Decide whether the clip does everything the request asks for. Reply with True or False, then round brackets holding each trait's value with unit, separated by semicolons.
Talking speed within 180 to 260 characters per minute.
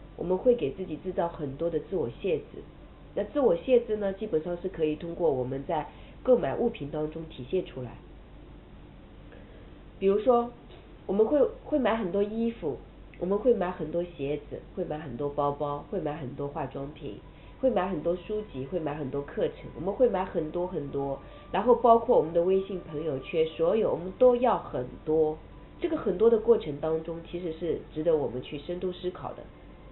False (275 characters per minute)